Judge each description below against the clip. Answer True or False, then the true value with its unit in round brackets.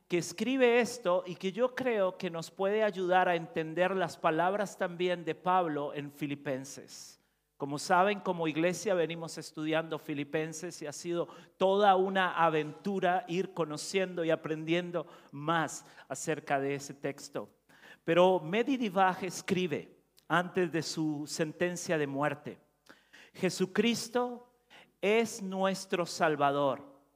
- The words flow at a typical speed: False (120 wpm)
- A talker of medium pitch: True (175 Hz)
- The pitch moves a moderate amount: True (3.3 semitones)